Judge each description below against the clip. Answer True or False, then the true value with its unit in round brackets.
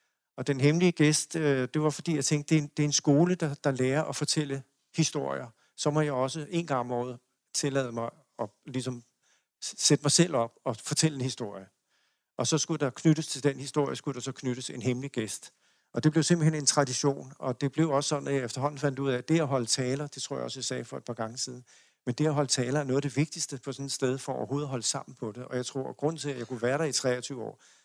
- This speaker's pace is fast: True (265 wpm)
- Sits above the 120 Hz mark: True (140 Hz)